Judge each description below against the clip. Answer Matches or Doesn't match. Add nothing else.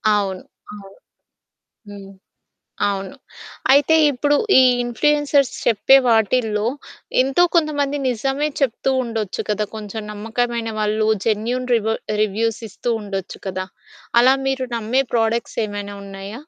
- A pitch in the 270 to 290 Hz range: Doesn't match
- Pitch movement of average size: Matches